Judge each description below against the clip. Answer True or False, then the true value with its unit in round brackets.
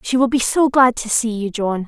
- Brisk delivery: True (290 wpm)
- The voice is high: True (235 Hz)